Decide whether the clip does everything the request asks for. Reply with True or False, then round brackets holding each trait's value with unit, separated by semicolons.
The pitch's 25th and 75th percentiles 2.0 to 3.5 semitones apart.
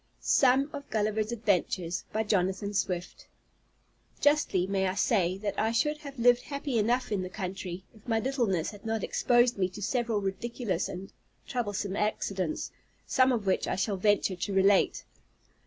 False (4.0 semitones)